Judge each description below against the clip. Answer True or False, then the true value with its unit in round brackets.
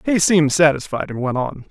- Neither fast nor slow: False (210 wpm)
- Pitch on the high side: False (150 Hz)